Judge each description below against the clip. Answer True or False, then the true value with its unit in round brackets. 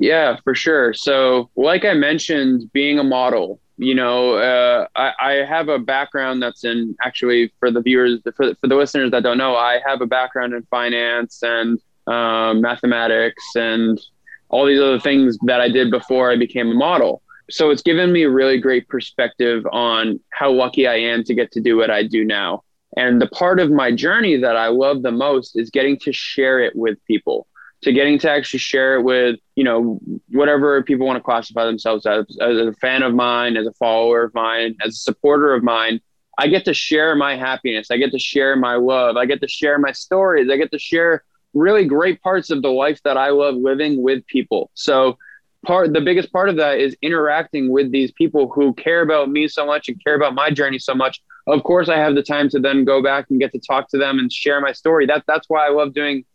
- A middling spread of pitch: True (3.2 semitones)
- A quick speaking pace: True (225 wpm)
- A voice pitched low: True (130 Hz)